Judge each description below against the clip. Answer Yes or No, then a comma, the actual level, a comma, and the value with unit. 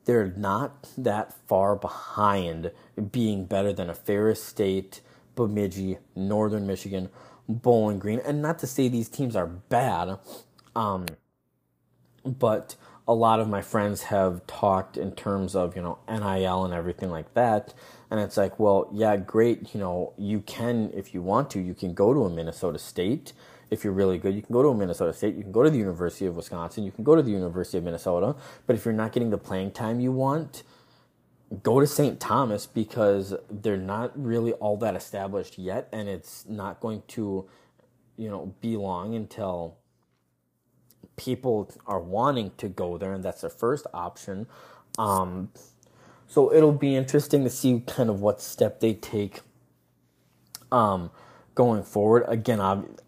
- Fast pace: No, average, 170 wpm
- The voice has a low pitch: Yes, low, 105 Hz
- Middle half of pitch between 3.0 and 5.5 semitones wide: Yes, average, 3.6 semitones